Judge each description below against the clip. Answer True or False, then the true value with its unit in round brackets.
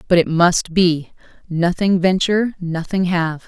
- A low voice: False (175 Hz)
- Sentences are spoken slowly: True (105 wpm)